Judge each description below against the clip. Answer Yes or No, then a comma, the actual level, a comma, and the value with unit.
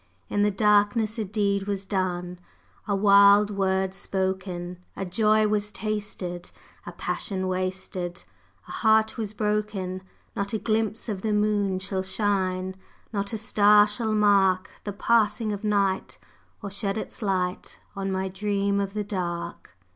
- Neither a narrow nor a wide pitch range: No, narrow, 1.9 semitones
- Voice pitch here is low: No, high, 200 Hz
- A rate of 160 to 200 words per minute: No, average, 145 wpm